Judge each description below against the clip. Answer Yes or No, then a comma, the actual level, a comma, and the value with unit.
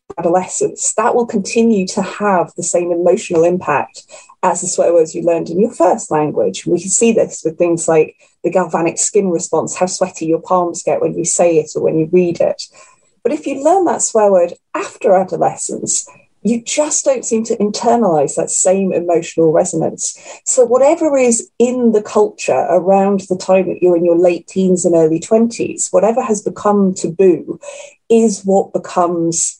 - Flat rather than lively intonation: No, average, 5.1 semitones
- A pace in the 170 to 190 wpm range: Yes, average, 180 wpm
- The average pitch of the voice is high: Yes, high, 195 Hz